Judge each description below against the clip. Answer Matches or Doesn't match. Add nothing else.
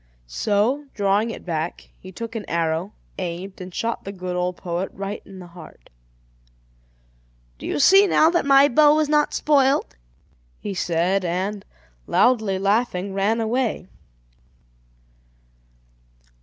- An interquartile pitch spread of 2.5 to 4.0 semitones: Doesn't match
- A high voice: Matches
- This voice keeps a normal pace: Doesn't match